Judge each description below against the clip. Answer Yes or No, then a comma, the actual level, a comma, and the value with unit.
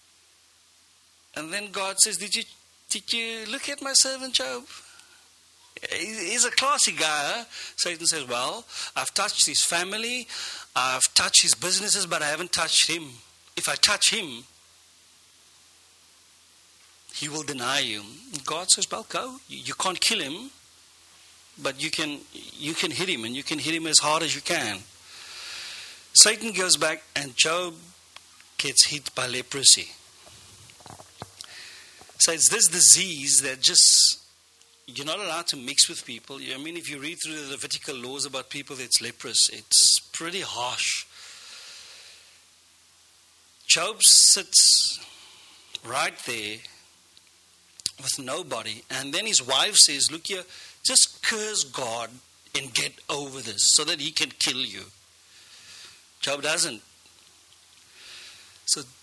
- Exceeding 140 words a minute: No, slow, 135 wpm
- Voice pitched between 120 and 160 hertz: Yes, medium, 140 Hz